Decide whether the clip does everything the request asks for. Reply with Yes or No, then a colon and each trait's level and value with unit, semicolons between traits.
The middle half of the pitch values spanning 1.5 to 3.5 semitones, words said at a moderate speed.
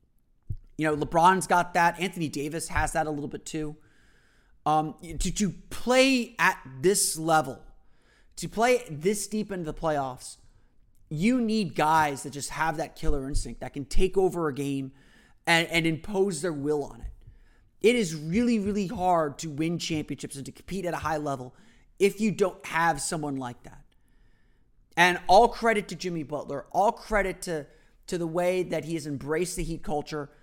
No: average, 4.3 semitones; average, 180 wpm